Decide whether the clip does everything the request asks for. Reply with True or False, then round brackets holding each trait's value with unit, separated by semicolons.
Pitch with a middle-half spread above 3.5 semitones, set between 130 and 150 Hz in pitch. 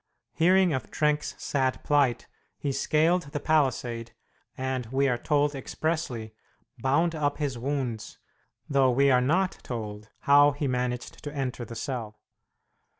False (3.2 semitones; 135 Hz)